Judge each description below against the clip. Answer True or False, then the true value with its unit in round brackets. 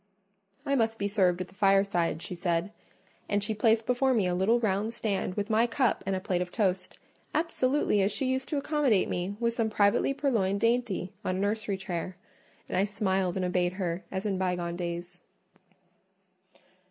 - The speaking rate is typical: True (185 wpm)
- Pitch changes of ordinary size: True (3.7 semitones)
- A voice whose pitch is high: True (200 Hz)